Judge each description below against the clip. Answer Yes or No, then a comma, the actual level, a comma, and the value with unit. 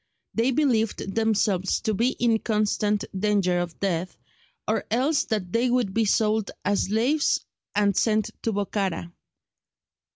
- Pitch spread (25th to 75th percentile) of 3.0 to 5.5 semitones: No, narrow, 2.6 semitones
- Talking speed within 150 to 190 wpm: No, slow, 135 wpm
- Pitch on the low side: No, high, 215 Hz